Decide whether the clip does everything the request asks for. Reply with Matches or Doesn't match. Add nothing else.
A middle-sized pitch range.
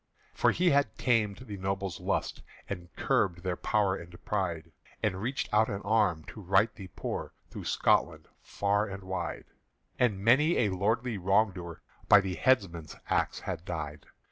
Matches